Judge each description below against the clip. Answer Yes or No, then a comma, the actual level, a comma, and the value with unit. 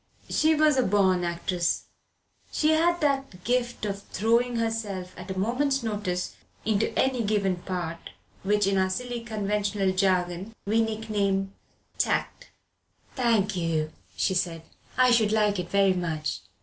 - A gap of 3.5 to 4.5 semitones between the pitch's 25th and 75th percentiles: Yes, average, 3.9 semitones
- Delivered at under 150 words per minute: Yes, average, 140 wpm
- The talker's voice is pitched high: Yes, high, 205 Hz